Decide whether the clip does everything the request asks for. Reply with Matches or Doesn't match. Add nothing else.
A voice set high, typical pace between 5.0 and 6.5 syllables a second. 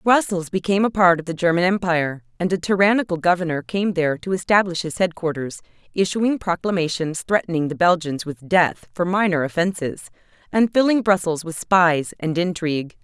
Doesn't match